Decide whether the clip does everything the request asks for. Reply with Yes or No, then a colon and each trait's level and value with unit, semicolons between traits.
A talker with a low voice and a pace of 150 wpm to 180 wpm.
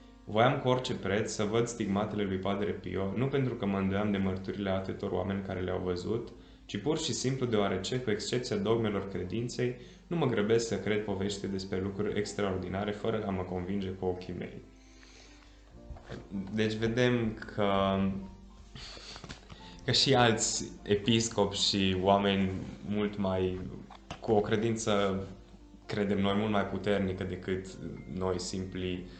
No: low, 100 Hz; average, 140 wpm